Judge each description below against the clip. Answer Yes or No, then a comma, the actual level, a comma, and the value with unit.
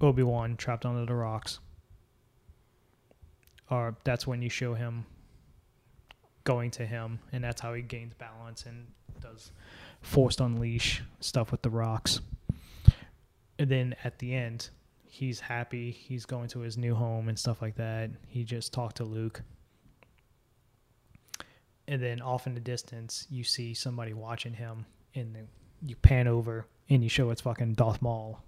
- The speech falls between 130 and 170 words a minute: Yes, average, 155 wpm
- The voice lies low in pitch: Yes, low, 120 Hz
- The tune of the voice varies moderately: No, narrow, 1.6 semitones